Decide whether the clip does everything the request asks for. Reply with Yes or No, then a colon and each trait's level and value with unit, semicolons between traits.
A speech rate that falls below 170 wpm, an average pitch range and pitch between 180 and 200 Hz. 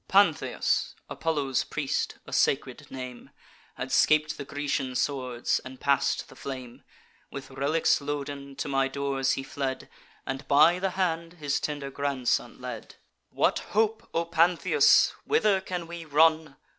No: average, 140 wpm; average, 3.6 semitones; medium, 145 Hz